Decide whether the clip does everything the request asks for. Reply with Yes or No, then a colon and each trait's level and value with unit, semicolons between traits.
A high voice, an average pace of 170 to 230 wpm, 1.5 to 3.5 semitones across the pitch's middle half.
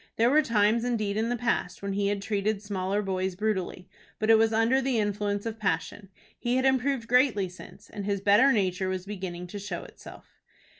Yes: high, 205 Hz; average, 200 wpm; average, 2.8 semitones